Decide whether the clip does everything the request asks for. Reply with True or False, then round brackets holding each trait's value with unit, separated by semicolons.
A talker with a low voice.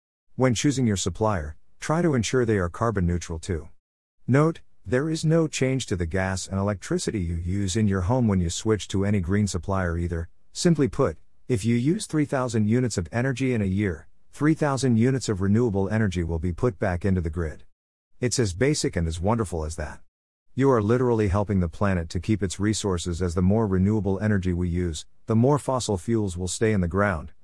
True (100 Hz)